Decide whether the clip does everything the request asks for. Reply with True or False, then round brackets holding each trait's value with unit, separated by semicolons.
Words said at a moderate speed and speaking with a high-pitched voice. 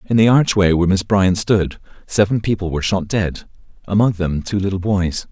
False (190 wpm; 95 Hz)